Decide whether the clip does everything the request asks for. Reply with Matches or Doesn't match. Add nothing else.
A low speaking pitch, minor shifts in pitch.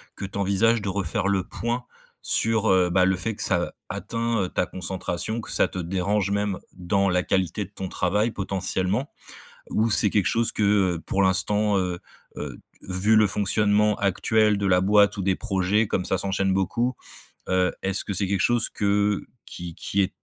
Matches